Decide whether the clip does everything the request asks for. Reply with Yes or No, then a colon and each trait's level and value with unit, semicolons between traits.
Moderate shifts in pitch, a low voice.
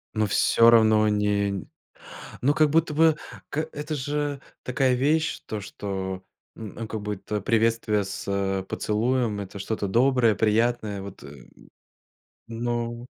Yes: average, 3.8 semitones; low, 110 Hz